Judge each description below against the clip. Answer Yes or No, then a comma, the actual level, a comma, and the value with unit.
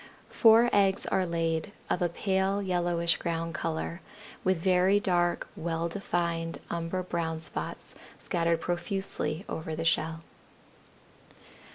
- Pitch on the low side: No, medium, 170 Hz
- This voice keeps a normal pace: No, slow, 115 wpm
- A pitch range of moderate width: No, narrow, 2.2 semitones